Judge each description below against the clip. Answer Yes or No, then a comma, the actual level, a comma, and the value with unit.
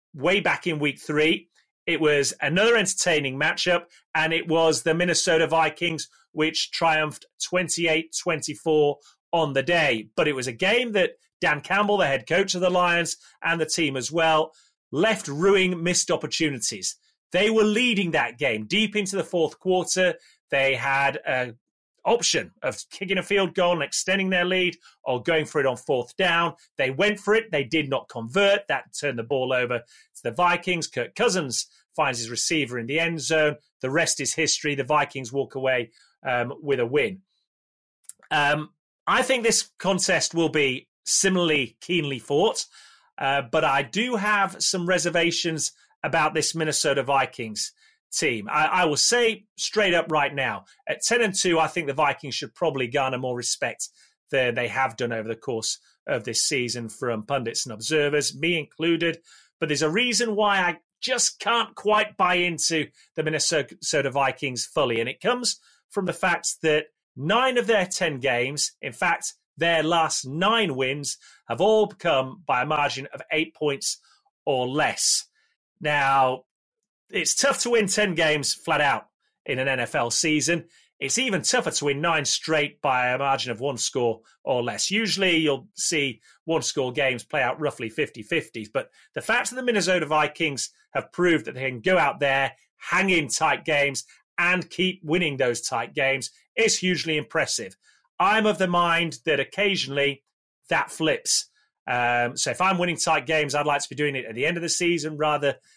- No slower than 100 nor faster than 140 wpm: No, average, 175 wpm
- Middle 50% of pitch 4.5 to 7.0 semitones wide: Yes, average, 4.9 semitones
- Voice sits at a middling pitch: Yes, medium, 160 Hz